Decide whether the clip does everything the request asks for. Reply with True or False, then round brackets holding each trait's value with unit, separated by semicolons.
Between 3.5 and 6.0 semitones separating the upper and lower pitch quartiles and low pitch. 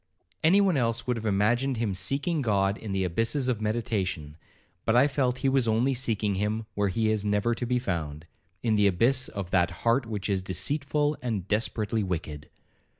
True (4.3 semitones; 110 Hz)